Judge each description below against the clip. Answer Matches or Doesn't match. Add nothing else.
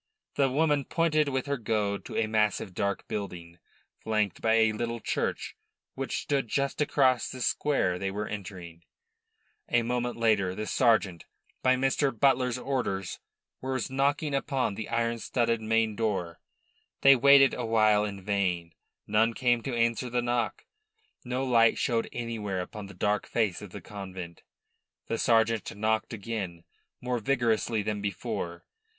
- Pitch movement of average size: Matches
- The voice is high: Doesn't match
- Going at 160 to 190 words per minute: Doesn't match